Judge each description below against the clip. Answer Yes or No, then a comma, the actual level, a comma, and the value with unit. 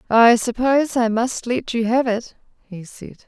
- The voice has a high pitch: Yes, high, 235 Hz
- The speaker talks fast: No, average, 185 wpm